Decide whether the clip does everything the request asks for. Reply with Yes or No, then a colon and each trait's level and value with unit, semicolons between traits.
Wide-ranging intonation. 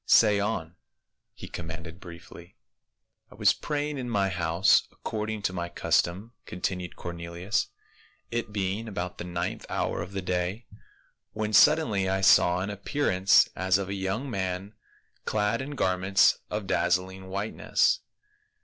No: average, 3.0 semitones